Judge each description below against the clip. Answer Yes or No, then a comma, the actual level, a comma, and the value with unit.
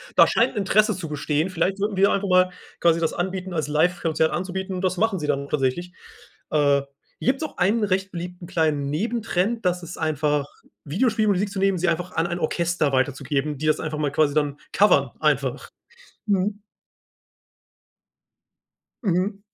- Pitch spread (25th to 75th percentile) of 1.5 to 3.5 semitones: No, average, 4.2 semitones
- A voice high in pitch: No, medium, 175 Hz